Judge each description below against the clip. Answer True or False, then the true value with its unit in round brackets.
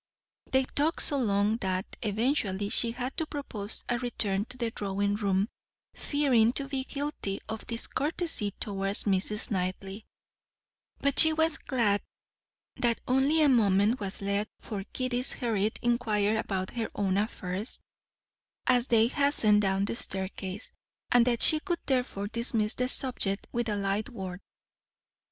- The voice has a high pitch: True (220 Hz)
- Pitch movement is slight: False (4.2 semitones)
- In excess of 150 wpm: False (145 wpm)